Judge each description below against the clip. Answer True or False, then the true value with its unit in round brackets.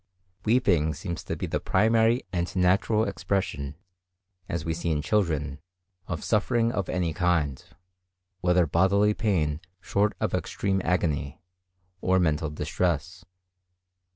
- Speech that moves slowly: True (125 wpm)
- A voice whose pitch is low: True (90 Hz)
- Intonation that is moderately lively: True (4.2 semitones)